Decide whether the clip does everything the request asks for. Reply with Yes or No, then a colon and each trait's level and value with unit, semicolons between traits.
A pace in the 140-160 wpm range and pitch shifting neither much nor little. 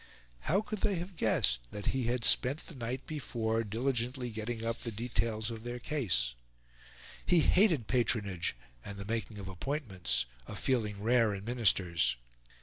Yes: average, 155 wpm; average, 4.1 semitones